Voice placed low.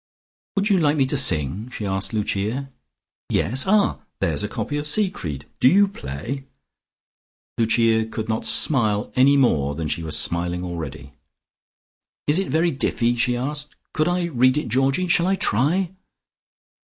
Yes: low, 125 Hz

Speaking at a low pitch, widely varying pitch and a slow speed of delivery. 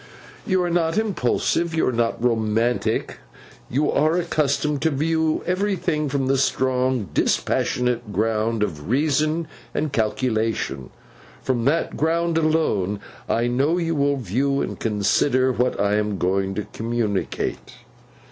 Yes: low, 130 Hz; wide, 5.9 semitones; slow, 130 wpm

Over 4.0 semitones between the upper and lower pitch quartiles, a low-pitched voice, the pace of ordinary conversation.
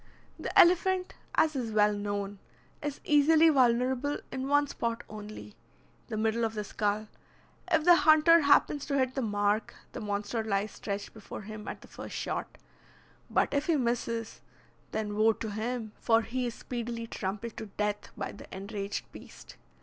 No: average, 4.8 semitones; high, 230 Hz; average, 165 wpm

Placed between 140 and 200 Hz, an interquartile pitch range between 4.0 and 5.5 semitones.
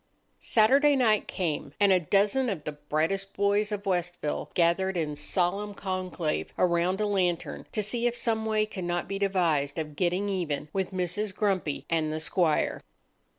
No: medium, 185 Hz; average, 3.4 semitones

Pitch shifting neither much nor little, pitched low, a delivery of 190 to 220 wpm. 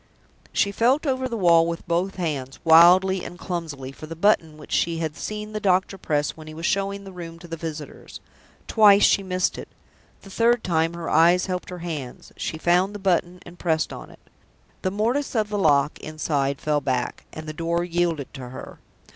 No: average, 3.6 semitones; medium, 170 Hz; average, 200 wpm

